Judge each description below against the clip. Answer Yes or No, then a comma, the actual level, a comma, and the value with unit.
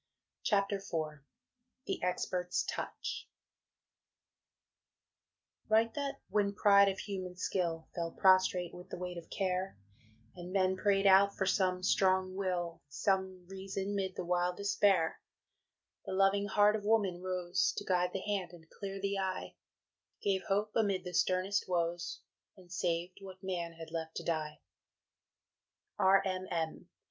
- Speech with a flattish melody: Yes, narrow, 1.9 semitones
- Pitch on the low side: No, medium, 185 Hz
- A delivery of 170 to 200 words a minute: No, average, 140 wpm